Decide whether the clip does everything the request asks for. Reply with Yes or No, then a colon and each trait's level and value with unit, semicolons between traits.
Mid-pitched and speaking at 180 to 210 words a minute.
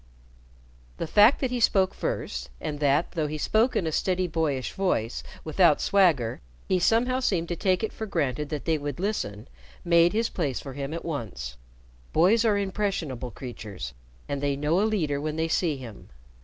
Yes: medium, 160 Hz; average, 185 wpm